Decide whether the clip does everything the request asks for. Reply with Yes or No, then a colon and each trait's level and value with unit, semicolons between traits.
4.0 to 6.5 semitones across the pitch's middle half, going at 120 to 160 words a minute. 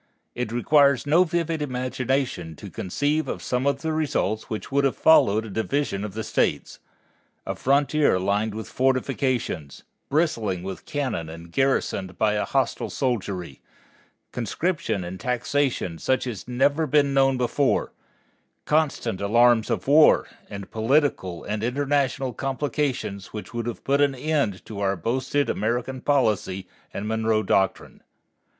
Yes: average, 5.2 semitones; average, 145 wpm